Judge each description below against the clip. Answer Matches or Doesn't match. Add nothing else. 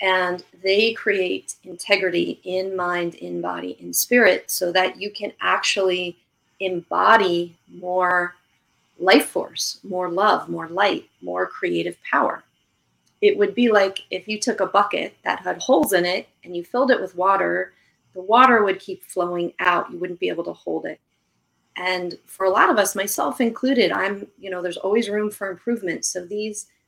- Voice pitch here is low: Doesn't match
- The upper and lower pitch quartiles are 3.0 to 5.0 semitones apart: Doesn't match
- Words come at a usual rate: Matches